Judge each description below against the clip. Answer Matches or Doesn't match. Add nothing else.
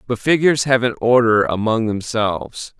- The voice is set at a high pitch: Doesn't match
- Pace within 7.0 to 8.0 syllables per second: Doesn't match